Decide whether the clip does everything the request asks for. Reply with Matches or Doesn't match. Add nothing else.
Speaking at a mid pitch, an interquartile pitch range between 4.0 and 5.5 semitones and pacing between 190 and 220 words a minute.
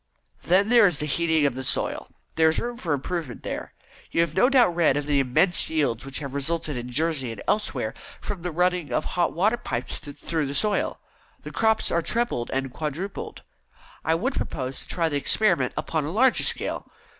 Matches